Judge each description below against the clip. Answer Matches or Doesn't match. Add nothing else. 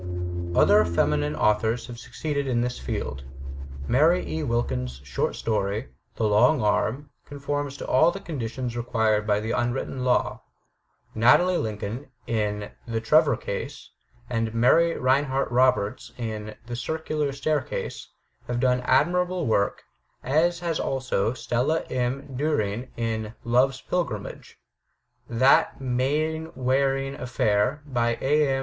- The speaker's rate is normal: Doesn't match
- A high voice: Doesn't match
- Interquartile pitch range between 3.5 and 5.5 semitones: Matches